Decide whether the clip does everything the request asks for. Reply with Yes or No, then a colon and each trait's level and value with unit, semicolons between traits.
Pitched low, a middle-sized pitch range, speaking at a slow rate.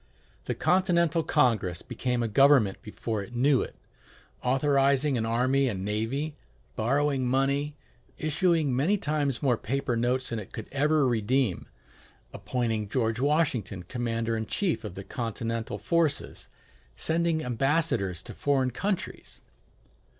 Yes: low, 130 Hz; average, 4.4 semitones; slow, 130 wpm